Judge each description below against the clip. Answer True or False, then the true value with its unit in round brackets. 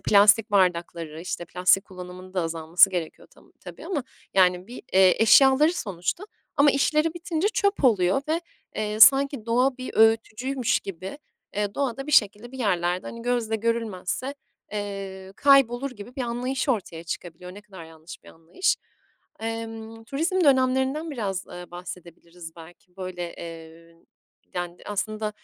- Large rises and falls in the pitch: True (6.2 semitones)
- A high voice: True (210 Hz)